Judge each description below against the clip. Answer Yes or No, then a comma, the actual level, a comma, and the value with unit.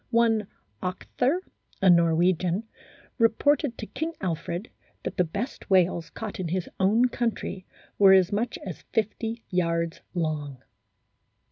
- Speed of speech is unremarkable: No, slow, 125 wpm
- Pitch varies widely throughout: No, average, 4.9 semitones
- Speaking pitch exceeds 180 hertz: Yes, high, 190 Hz